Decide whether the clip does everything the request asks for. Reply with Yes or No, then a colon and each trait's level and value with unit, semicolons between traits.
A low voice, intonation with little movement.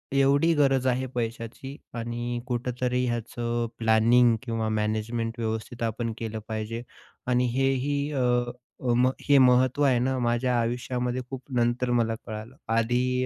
Yes: low, 120 Hz; narrow, 1.8 semitones